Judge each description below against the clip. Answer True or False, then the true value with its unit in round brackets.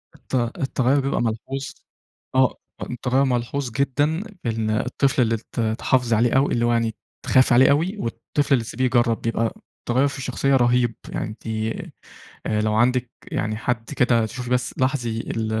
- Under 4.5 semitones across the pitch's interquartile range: True (2.6 semitones)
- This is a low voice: True (125 Hz)